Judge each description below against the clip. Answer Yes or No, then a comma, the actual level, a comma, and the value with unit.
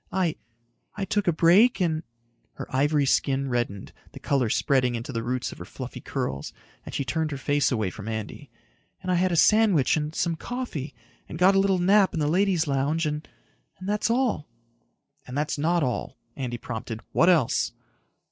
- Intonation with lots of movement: Yes, wide, 5.9 semitones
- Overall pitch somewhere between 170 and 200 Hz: No, medium, 155 Hz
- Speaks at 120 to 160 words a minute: No, average, 185 wpm